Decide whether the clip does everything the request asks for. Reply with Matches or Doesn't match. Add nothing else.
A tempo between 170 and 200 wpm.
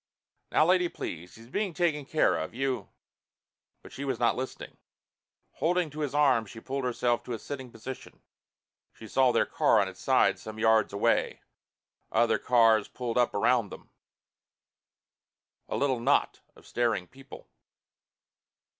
Doesn't match